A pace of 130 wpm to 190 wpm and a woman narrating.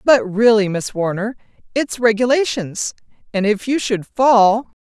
Yes: slow, 135 wpm; female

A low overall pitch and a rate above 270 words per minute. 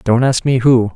No: low, 125 Hz; fast, 255 wpm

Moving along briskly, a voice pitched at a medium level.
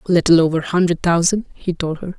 Yes: fast, 245 wpm; medium, 170 Hz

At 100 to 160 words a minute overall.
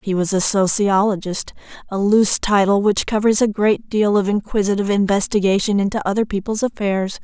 Yes: average, 150 wpm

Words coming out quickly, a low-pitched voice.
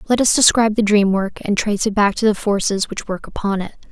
No: fast, 260 wpm; high, 210 Hz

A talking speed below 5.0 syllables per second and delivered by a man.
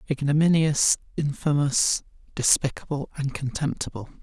Yes: 4.7 syllables/s; male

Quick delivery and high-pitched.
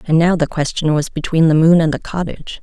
No: fast, 250 wpm; medium, 160 Hz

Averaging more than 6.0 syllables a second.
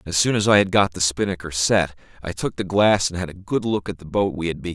Yes: 6.4 syllables/s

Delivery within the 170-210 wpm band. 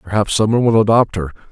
No: fast, 240 wpm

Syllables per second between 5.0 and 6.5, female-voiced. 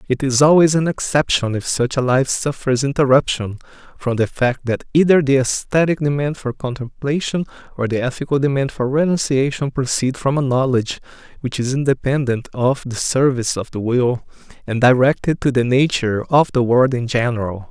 No: 5.3 syllables/s; male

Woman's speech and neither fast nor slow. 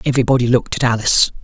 No: male; average, 165 wpm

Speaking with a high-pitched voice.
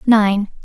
Yes: high, 210 Hz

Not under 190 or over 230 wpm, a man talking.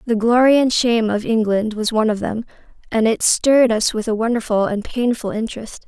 No: fast, 205 wpm; female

